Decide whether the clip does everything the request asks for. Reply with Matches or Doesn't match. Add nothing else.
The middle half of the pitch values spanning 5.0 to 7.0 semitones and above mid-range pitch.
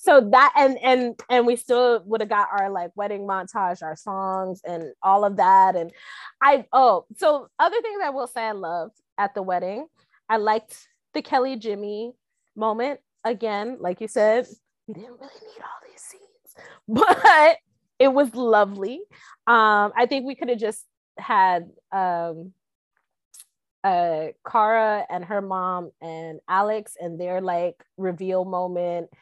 Matches